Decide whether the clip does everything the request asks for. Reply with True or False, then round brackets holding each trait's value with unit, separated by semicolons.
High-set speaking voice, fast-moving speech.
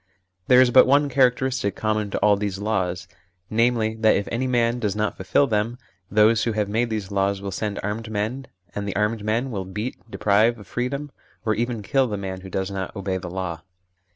False (110 Hz; 210 wpm)